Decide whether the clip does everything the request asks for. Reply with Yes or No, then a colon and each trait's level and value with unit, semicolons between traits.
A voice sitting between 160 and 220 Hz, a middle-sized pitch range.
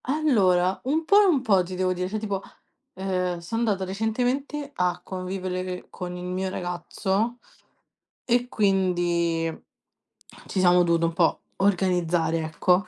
Yes: medium, 185 Hz; average, 3.4 semitones